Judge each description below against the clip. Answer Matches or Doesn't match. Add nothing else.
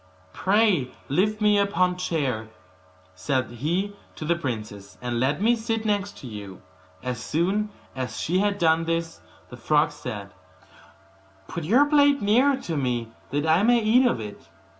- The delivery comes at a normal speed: Matches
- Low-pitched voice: Doesn't match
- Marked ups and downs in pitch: Matches